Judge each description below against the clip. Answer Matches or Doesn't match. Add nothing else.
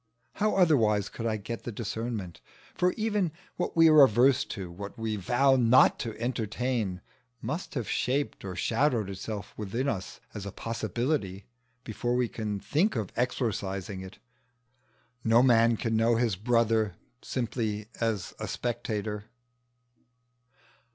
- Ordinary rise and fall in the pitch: Matches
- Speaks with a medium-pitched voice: Doesn't match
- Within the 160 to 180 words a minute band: Doesn't match